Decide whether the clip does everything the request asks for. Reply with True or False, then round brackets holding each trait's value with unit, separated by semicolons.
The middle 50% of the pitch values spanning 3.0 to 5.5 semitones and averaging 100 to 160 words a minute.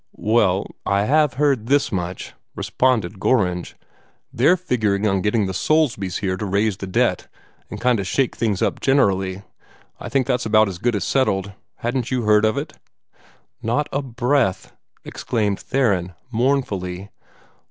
True (5.1 semitones; 150 wpm)